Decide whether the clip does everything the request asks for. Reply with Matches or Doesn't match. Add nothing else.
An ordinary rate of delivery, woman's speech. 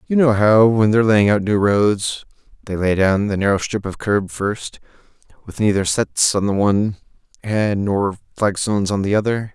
Doesn't match